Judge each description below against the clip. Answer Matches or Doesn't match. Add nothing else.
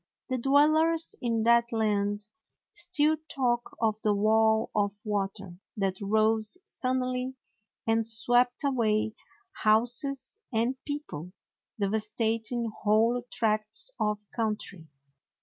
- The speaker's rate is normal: Doesn't match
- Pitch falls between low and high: Doesn't match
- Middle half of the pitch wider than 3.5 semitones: Doesn't match